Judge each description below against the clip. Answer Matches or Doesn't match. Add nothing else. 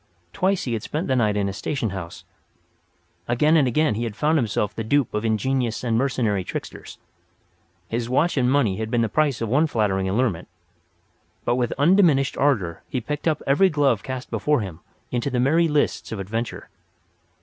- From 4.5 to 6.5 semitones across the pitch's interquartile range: Matches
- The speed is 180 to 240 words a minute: Matches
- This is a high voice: Doesn't match